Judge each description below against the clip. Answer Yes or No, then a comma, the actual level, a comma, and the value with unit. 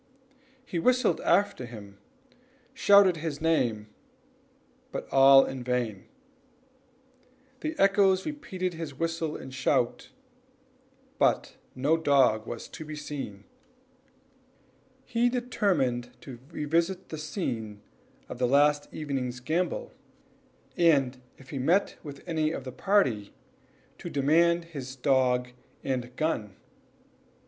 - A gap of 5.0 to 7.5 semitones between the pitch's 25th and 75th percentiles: Yes, average, 5.3 semitones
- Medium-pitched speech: Yes, medium, 145 Hz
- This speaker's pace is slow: Yes, slow, 115 wpm